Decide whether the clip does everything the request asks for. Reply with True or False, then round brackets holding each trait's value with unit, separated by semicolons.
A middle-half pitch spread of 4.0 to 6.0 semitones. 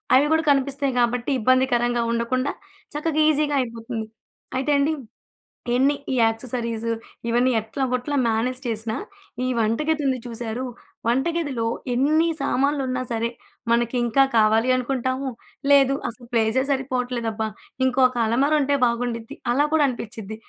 False (2.9 semitones)